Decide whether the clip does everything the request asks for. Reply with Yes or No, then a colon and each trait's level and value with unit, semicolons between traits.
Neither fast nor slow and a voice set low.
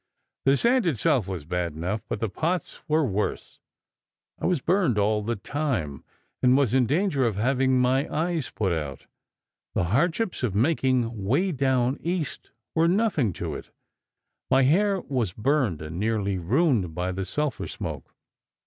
Yes: average, 160 wpm; low, 130 Hz